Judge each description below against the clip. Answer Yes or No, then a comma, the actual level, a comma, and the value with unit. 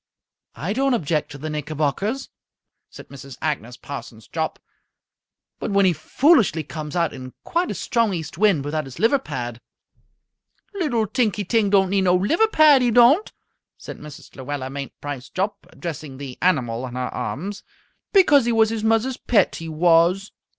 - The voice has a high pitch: No, medium, 175 Hz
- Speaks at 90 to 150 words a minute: No, average, 165 wpm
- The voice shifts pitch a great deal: Yes, wide, 7.9 semitones